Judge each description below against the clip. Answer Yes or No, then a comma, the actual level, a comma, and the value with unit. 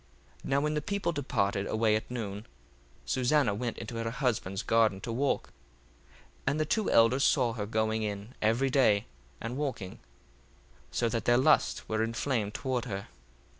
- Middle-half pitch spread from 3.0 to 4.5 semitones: Yes, average, 3.6 semitones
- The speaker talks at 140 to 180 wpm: Yes, average, 170 wpm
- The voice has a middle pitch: No, low, 115 Hz